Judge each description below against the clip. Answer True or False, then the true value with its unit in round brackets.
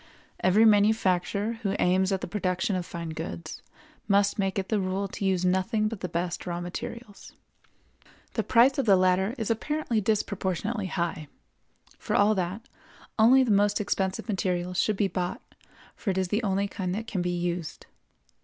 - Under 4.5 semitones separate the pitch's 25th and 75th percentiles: True (2.9 semitones)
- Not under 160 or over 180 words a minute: True (170 wpm)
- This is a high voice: True (195 Hz)